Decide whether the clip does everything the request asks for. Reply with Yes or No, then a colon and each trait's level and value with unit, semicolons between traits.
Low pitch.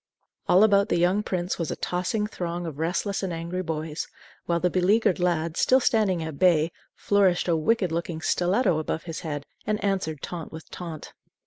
No: medium, 175 Hz